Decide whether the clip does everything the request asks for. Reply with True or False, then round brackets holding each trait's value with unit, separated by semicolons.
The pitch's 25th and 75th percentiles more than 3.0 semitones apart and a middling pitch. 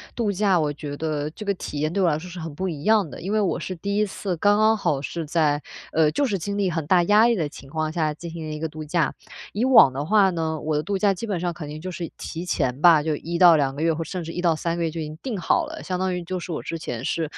True (3.6 semitones; 170 Hz)